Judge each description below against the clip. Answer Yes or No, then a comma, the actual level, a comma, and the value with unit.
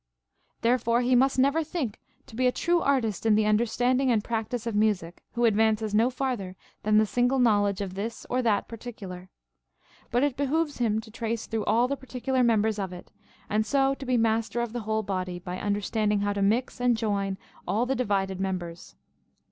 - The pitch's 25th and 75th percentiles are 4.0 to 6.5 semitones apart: No, average, 3.4 semitones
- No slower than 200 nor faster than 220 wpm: Yes, fast, 205 wpm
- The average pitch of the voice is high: Yes, high, 225 Hz